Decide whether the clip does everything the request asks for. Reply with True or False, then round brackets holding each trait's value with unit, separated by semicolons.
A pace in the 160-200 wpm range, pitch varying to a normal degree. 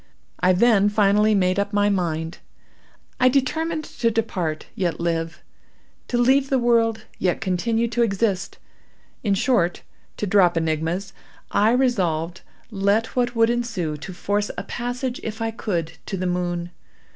False (140 wpm; 4.8 semitones)